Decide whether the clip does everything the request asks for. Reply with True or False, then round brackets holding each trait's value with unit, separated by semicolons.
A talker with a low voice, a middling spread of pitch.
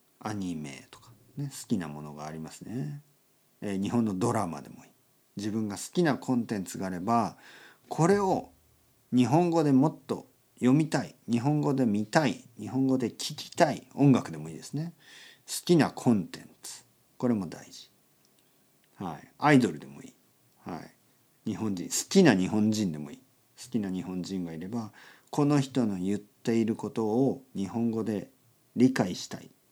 True (120 Hz; 4.7 semitones)